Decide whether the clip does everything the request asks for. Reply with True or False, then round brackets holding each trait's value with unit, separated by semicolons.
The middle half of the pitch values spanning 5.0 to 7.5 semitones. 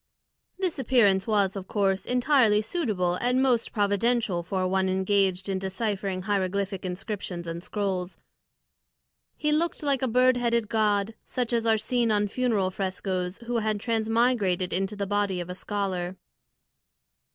False (3.8 semitones)